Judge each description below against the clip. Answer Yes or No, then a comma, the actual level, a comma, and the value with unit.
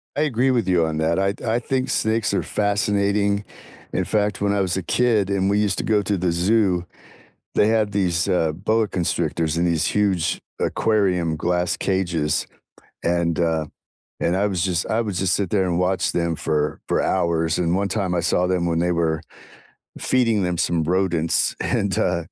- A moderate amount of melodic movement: Yes, average, 3.3 semitones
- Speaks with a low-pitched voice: Yes, very low, 95 Hz